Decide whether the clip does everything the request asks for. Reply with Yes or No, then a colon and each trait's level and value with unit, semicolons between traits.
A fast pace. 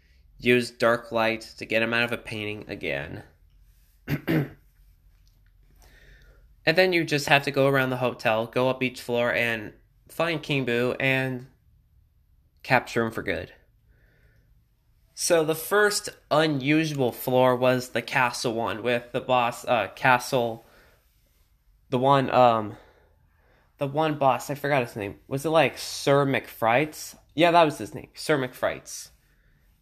No: average, 140 wpm